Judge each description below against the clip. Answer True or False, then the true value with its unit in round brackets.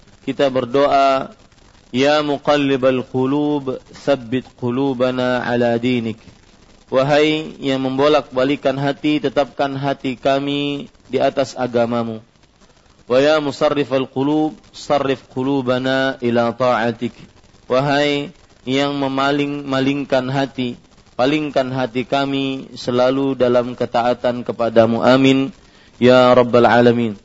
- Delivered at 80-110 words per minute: True (90 wpm)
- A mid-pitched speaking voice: False (130 Hz)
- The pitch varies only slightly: True (2.3 semitones)